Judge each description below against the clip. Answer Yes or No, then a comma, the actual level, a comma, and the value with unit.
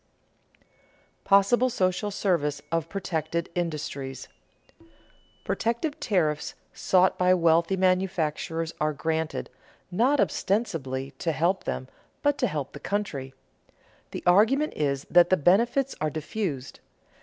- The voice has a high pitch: No, medium, 175 Hz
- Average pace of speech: No, slow, 115 wpm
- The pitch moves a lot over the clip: No, average, 4.6 semitones